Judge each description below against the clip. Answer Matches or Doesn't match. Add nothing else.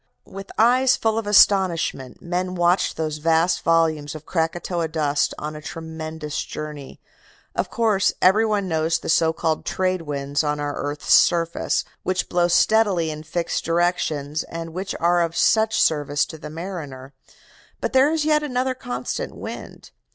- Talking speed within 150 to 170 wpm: Matches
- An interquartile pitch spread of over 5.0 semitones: Doesn't match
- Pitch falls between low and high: Matches